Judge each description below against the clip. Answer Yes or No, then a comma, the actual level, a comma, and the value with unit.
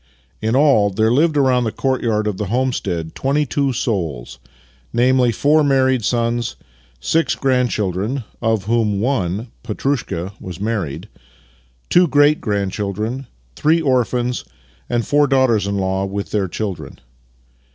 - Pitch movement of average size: Yes, average, 4.7 semitones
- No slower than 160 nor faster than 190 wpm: No, average, 140 wpm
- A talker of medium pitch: No, low, 115 Hz